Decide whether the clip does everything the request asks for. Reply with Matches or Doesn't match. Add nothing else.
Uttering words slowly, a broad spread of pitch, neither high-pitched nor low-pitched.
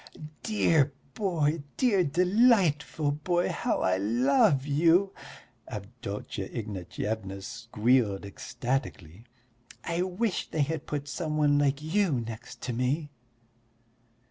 Matches